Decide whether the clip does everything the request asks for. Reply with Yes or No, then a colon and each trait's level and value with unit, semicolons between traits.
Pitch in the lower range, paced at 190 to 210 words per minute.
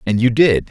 No: low, 115 Hz; fast, 255 wpm